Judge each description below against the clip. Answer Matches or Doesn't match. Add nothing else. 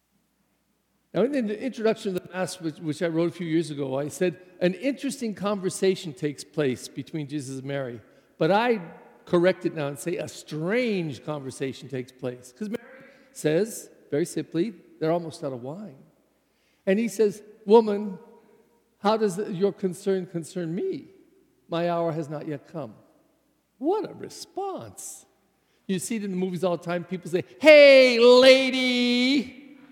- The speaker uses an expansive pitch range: Matches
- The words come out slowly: Doesn't match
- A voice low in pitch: Doesn't match